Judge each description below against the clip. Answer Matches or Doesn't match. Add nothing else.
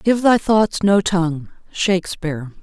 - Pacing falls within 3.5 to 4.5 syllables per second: Matches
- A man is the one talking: Doesn't match